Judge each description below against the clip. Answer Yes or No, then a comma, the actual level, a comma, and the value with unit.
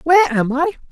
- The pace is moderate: Yes, average, 195 wpm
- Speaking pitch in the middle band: No, high, 235 Hz